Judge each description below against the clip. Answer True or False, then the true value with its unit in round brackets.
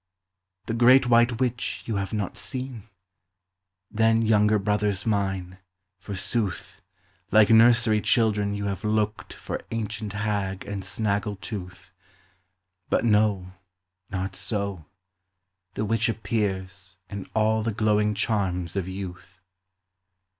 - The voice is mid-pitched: False (105 Hz)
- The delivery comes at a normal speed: False (115 wpm)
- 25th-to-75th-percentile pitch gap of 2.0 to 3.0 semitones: True (2.5 semitones)